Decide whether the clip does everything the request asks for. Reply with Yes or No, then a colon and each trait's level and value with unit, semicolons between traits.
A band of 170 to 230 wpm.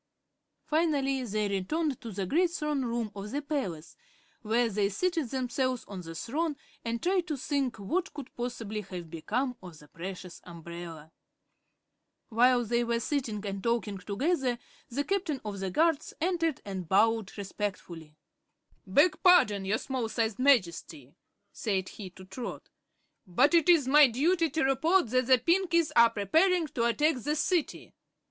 No: average, 155 wpm